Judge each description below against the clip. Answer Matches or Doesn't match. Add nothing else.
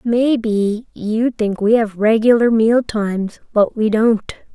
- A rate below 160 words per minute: Matches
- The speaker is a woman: Matches